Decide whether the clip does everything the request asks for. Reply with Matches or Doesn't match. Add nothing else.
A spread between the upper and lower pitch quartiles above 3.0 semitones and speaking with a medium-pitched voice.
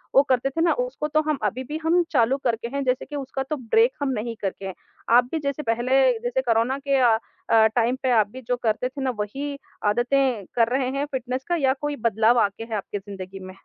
Doesn't match